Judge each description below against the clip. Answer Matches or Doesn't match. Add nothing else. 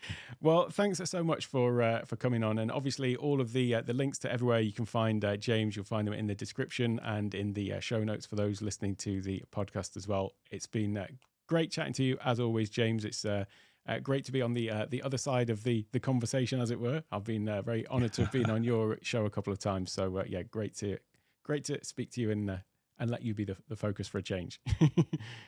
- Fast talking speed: Matches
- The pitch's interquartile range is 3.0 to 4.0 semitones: Matches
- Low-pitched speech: Matches